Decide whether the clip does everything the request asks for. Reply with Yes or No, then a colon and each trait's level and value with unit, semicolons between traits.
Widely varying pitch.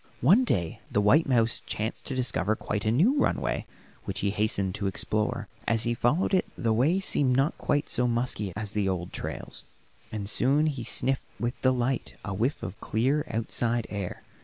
No: average, 4.3 semitones